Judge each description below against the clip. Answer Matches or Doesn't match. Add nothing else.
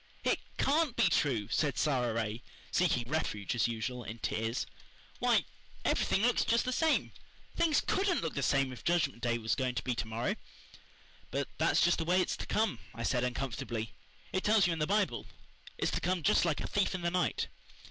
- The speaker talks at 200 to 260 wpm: Matches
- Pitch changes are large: Matches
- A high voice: Doesn't match